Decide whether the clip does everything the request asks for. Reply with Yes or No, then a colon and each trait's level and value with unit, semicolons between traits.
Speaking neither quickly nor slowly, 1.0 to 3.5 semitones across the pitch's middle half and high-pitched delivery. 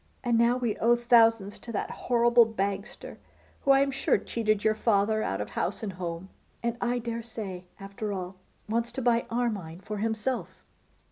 Yes: average, 180 wpm; average, 2.9 semitones; high, 225 Hz